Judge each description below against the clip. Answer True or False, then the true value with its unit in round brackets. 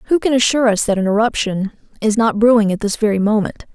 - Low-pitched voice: False (220 Hz)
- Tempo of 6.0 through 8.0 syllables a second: True (6.4 syllables/s)